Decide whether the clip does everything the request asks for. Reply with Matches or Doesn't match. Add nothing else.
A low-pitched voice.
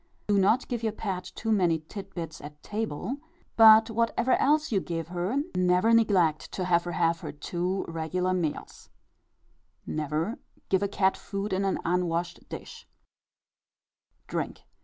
Doesn't match